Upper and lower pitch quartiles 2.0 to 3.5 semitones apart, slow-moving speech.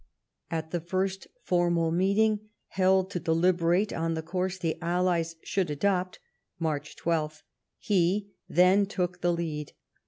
Yes: narrow, 2.4 semitones; slow, 130 wpm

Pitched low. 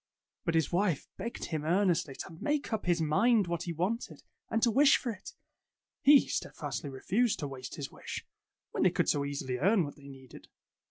No: medium, 170 Hz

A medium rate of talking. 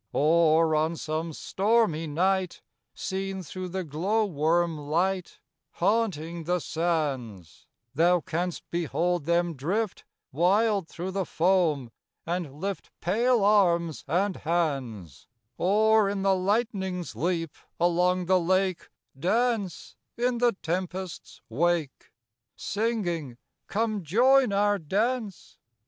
No: slow, 110 wpm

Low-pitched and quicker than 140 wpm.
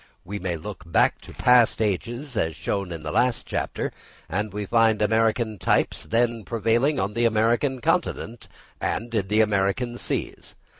Yes: low, 110 Hz; average, 160 wpm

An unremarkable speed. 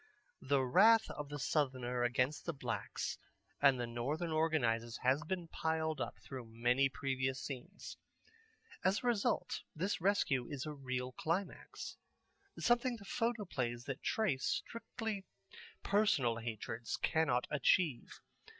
No: slow, 125 wpm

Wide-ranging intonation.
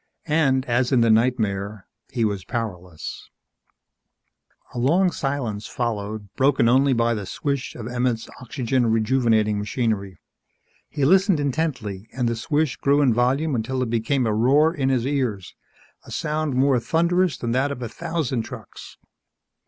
No: average, 4.0 semitones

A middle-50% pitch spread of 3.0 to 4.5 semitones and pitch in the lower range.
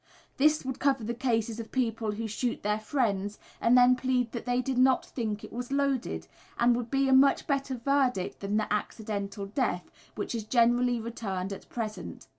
No: average, 3.3 semitones; high, 235 Hz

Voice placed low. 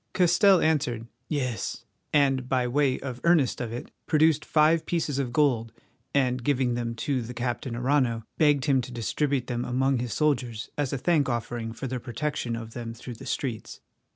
Yes: low, 130 Hz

